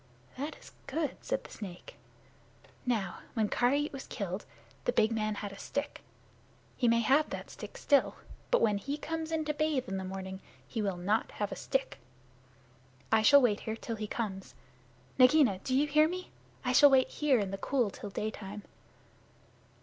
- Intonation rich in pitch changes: Yes, wide, 5.9 semitones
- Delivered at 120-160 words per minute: No, average, 180 wpm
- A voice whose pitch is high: Yes, high, 235 Hz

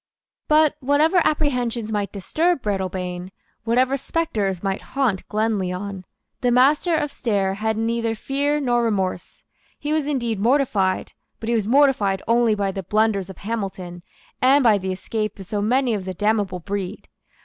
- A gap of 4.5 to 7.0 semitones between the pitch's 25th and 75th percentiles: Yes, average, 5.2 semitones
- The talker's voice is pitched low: No, high, 220 Hz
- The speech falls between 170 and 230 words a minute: No, average, 155 wpm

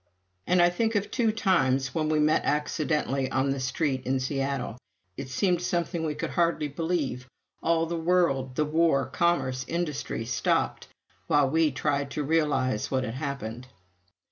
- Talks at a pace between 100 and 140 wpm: No, average, 160 wpm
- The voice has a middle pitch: Yes, medium, 150 Hz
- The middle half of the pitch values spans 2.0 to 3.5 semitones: No, average, 4.0 semitones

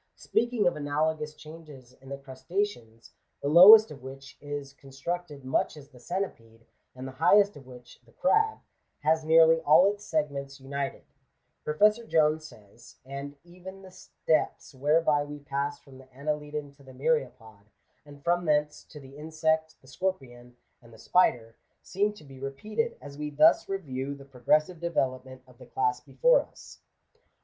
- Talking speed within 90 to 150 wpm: No, average, 165 wpm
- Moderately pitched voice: Yes, medium, 145 Hz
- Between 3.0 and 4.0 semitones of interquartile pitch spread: Yes, average, 3.7 semitones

